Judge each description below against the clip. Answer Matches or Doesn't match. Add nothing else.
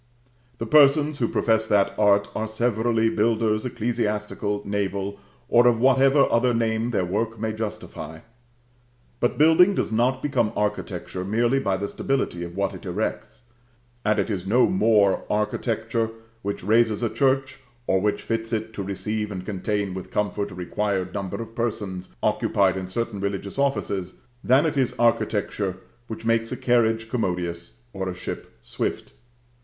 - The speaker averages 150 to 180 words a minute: Matches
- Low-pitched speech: Matches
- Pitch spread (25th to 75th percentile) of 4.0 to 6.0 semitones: Doesn't match